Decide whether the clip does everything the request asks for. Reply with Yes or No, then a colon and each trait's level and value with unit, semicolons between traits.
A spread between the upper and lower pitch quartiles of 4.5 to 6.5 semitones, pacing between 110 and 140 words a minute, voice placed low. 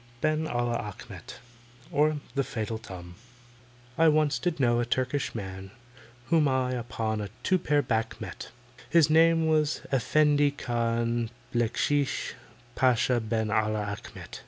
Yes: average, 4.8 semitones; slow, 135 wpm; low, 125 Hz